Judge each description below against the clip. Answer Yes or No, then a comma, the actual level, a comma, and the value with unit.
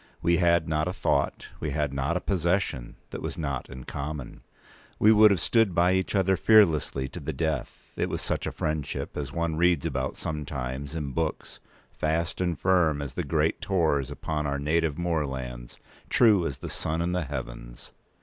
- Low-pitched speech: Yes, very low, 80 Hz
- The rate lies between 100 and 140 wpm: No, average, 185 wpm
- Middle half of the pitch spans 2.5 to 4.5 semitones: Yes, average, 3.8 semitones